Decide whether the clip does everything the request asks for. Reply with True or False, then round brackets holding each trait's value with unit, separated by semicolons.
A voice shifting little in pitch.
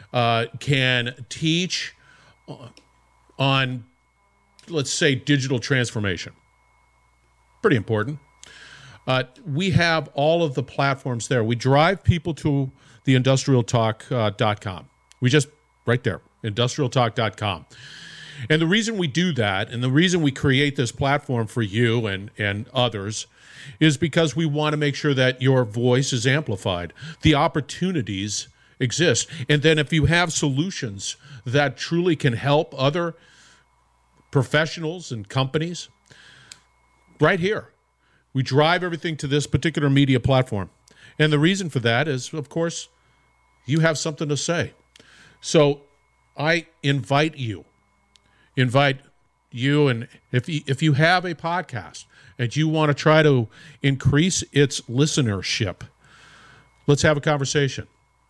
False (4.1 semitones)